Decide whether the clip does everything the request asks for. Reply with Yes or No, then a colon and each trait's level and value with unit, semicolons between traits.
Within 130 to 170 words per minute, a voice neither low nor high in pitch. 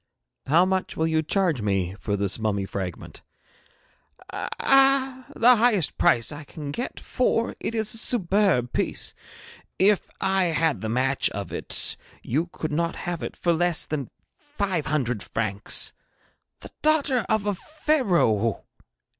Yes: average, 145 wpm; medium, 170 Hz